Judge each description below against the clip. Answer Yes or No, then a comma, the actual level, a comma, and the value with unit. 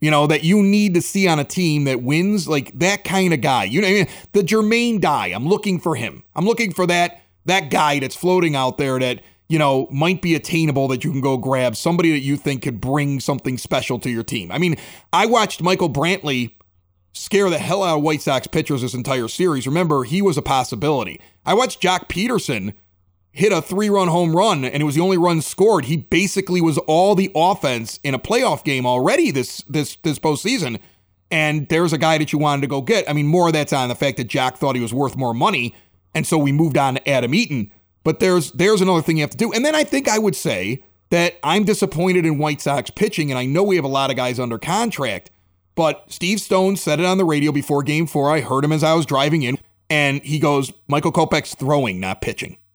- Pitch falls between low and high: Yes, medium, 150 Hz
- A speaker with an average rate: No, fast, 235 wpm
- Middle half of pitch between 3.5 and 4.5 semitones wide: No, average, 5.1 semitones